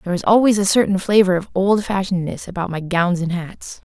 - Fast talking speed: Yes, fast, 215 wpm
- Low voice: No, high, 190 Hz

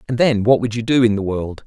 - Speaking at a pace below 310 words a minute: No, fast, 325 wpm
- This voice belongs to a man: Yes, male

